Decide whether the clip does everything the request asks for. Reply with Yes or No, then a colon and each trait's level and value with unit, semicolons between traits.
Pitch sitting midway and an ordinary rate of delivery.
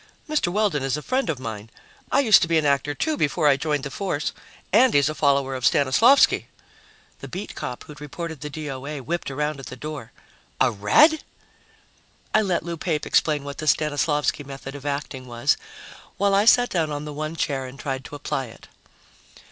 Yes: medium, 150 Hz; average, 195 wpm